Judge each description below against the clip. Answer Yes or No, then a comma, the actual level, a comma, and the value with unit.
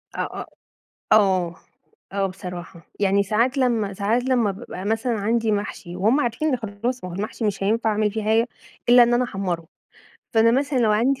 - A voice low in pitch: No, high, 220 Hz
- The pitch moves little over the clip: No, average, 3.4 semitones